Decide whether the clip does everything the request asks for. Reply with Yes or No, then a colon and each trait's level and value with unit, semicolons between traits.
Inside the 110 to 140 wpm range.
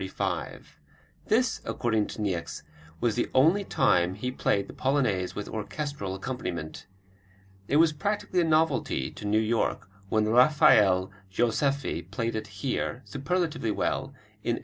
Yes: slow, 135 wpm